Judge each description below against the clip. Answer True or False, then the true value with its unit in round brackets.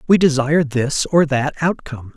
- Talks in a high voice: False (145 Hz)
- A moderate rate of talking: True (165 wpm)